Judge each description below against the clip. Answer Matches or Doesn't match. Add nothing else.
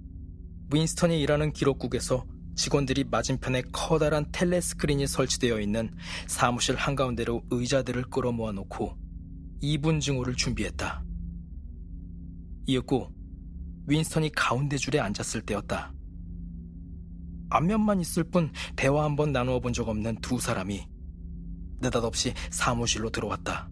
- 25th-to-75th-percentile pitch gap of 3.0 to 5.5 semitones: Doesn't match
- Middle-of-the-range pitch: Doesn't match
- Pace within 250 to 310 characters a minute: Matches